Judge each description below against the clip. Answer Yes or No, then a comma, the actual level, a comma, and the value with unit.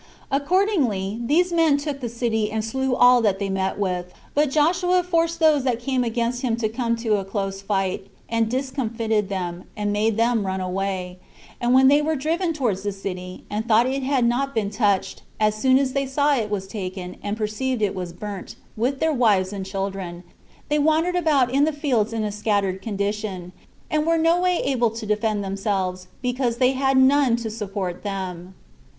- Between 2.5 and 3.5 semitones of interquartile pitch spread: No, wide, 5.4 semitones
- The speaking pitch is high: Yes, high, 225 Hz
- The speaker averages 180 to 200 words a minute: Yes, average, 195 wpm